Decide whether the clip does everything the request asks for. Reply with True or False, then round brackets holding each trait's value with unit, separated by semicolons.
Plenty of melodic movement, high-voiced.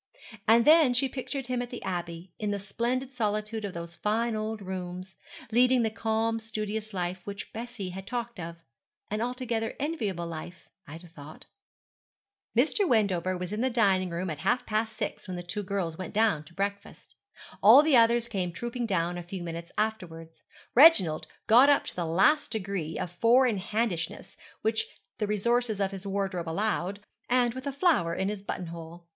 False (4.8 semitones; 205 Hz)